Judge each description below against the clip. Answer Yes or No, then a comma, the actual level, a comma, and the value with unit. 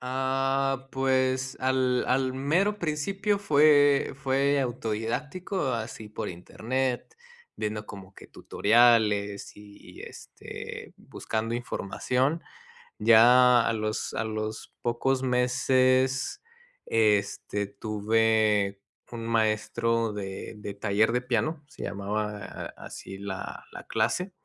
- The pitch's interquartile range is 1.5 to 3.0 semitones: No, average, 3.7 semitones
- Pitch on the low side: Yes, low, 120 Hz